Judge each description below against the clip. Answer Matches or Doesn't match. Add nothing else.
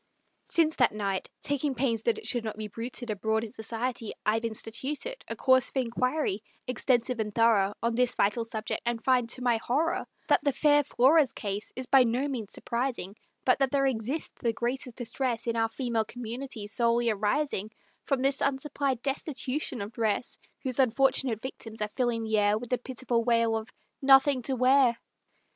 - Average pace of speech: Matches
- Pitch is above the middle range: Matches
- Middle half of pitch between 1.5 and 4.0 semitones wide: Matches